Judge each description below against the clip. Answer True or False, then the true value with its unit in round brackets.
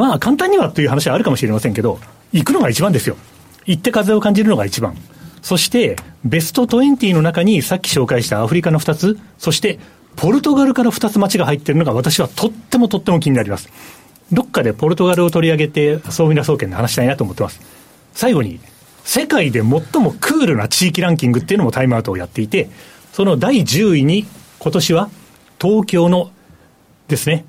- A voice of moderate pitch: True (165 Hz)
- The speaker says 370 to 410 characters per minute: True (400 characters per minute)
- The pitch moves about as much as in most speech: False (6.4 semitones)